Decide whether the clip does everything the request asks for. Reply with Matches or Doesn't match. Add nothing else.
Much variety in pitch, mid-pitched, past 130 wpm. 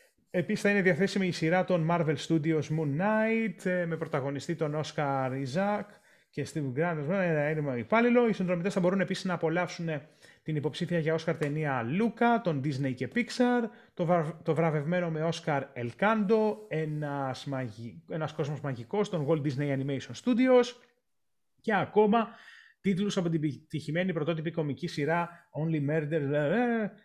Doesn't match